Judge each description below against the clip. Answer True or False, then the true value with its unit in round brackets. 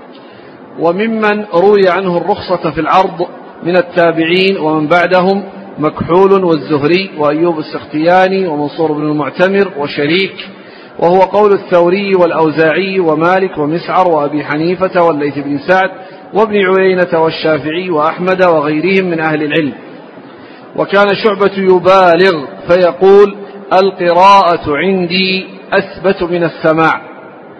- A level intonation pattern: False (3.0 semitones)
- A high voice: False (180 Hz)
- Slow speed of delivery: False (100 wpm)